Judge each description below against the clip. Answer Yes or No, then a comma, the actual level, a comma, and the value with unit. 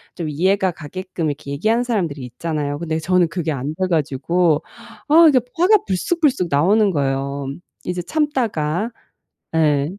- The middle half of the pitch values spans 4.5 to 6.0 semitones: Yes, wide, 5.4 semitones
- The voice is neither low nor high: Yes, medium, 170 Hz